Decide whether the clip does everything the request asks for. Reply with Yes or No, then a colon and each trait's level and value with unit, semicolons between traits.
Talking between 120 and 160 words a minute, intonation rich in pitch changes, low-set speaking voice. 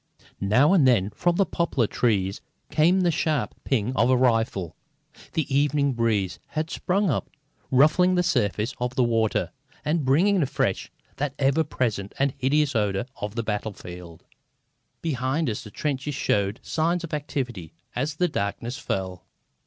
Yes: average, 155 wpm; wide, 6.2 semitones; low, 130 Hz